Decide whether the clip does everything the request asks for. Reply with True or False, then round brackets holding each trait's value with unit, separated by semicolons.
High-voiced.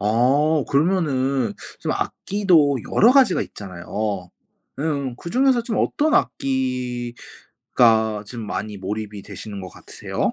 False (130 Hz)